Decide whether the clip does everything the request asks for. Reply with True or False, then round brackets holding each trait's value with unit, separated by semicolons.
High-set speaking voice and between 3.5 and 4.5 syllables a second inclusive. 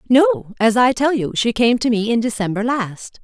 False (230 Hz; 4.9 syllables/s)